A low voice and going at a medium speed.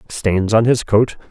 Yes: low, 105 Hz; average, 185 wpm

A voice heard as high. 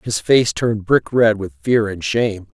No: low, 110 Hz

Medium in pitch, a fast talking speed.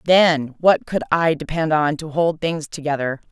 No: medium, 155 Hz; average, 180 wpm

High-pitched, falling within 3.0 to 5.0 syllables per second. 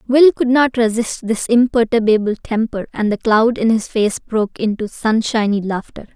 Yes: high, 225 Hz; 4.8 syllables/s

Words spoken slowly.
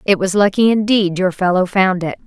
No: fast, 210 wpm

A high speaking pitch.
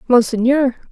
Yes: very high, 250 Hz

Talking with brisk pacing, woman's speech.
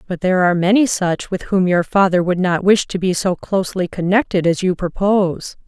Yes: fast, 210 wpm; female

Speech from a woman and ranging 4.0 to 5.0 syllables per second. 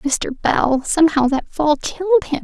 Yes: female; 4.2 syllables/s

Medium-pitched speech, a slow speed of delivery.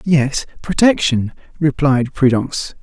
Yes: medium, 145 Hz; slow, 85 wpm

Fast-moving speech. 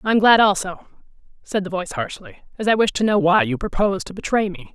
Yes: fast, 240 wpm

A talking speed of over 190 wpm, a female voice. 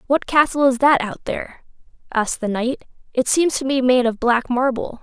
Yes: fast, 205 wpm; female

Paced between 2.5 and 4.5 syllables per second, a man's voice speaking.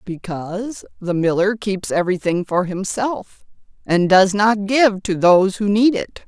No: 4.3 syllables/s; female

